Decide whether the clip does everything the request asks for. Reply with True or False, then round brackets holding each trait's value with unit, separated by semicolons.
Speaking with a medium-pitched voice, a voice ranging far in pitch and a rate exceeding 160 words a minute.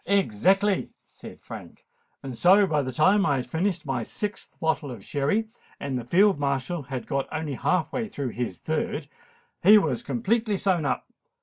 True (160 Hz; 6.8 semitones; 175 wpm)